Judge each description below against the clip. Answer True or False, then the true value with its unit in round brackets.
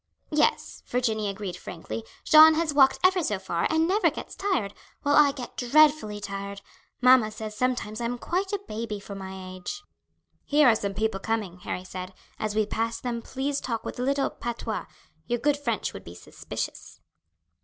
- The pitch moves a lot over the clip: True (6.1 semitones)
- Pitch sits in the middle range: False (230 Hz)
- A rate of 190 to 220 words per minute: False (180 wpm)